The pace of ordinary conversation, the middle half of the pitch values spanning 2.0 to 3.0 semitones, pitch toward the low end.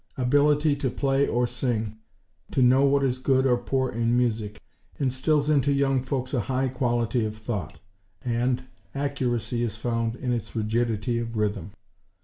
Yes: average, 155 wpm; narrow, 2.6 semitones; low, 125 Hz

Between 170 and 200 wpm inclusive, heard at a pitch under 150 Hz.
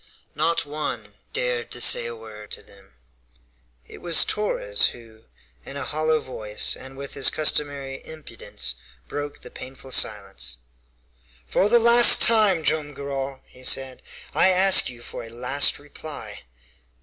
No: average, 145 wpm; low, 135 Hz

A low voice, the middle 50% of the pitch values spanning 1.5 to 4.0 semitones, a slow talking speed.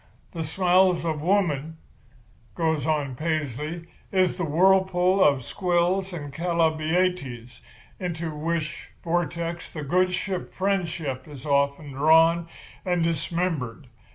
No: medium, 165 Hz; average, 3.1 semitones; slow, 110 wpm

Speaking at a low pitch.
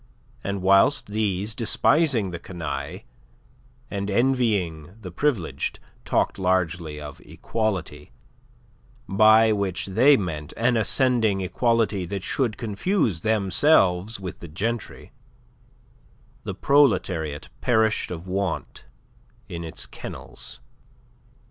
Yes: low, 100 Hz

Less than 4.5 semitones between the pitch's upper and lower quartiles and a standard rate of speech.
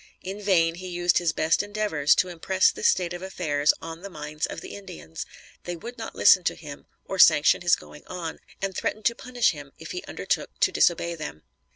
No: average, 3.4 semitones; fast, 210 wpm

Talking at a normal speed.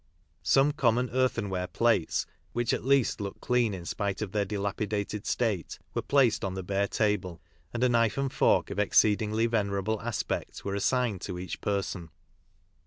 Yes: average, 165 wpm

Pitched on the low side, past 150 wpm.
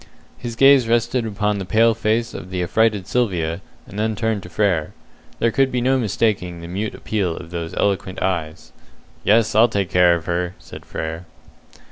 Yes: low, 100 Hz; average, 180 wpm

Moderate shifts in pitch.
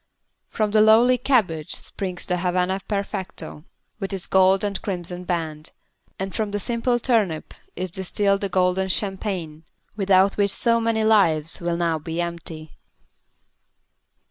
Yes: average, 3.2 semitones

